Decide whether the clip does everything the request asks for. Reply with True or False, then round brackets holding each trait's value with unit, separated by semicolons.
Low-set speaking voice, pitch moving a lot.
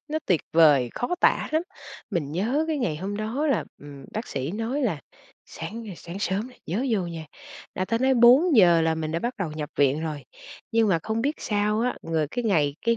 False (200 Hz; 6.7 semitones)